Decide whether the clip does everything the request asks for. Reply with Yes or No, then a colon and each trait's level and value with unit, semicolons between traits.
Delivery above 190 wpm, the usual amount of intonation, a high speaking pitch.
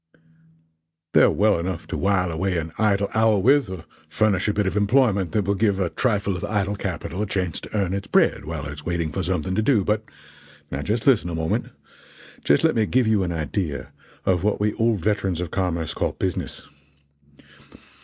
No: average, 200 wpm; average, 3.5 semitones; very low, 95 Hz